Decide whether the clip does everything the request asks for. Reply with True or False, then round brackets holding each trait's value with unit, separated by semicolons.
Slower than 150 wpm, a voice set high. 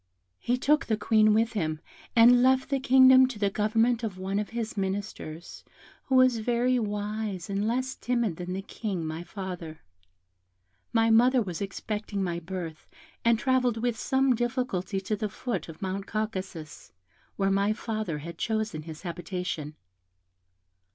False (155 wpm; 215 Hz)